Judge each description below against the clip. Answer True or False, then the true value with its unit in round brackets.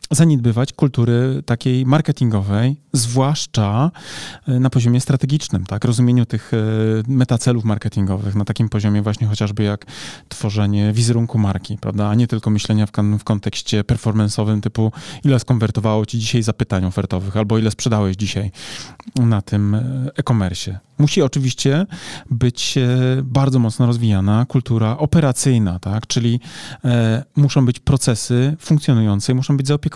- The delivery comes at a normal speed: True (125 wpm)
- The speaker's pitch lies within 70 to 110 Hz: False (120 Hz)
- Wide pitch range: False (3.8 semitones)